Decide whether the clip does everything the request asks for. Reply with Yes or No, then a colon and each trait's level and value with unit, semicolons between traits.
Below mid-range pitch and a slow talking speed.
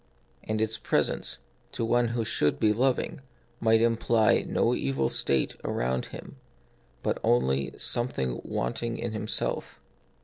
Yes: low, 110 Hz; slow, 130 wpm